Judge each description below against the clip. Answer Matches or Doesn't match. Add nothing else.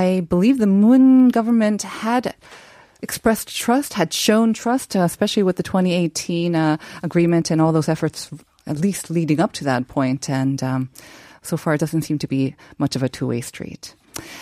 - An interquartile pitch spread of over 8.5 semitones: Doesn't match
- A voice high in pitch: Doesn't match